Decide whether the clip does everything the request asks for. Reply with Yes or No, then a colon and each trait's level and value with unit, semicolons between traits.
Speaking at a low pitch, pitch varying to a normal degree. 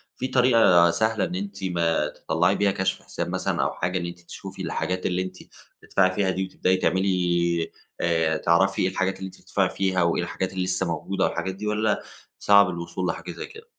No: very low, 95 Hz; narrow, 2.0 semitones